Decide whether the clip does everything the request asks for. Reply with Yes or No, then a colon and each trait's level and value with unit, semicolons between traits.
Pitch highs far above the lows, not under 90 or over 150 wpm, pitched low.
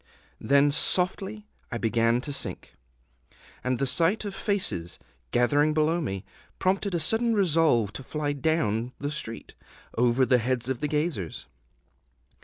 No: wide, 5.9 semitones; average, 140 wpm; medium, 145 Hz